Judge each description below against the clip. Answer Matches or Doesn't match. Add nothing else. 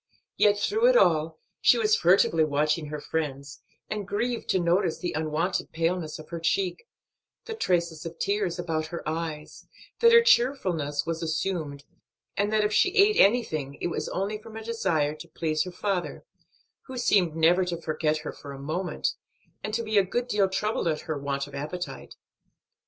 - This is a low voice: Doesn't match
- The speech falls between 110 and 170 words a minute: Doesn't match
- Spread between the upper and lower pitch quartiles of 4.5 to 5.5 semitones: Matches